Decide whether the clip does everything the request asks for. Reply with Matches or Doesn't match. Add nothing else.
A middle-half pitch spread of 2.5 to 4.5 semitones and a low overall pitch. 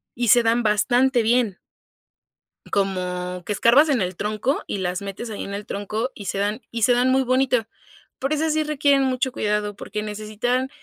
Doesn't match